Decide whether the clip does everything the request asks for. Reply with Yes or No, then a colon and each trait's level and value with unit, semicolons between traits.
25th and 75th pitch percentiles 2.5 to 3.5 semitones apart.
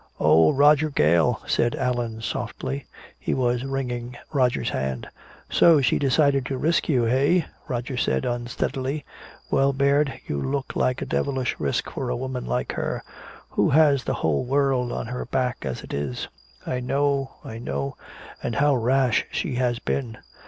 Yes: average, 2.9 semitones